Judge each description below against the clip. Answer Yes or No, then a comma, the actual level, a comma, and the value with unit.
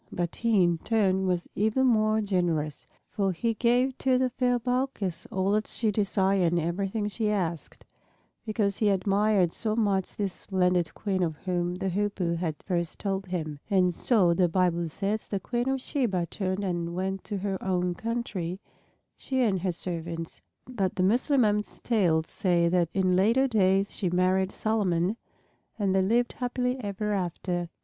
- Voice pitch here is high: Yes, high, 195 Hz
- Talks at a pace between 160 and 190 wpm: Yes, average, 165 wpm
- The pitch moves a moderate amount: Yes, average, 3.4 semitones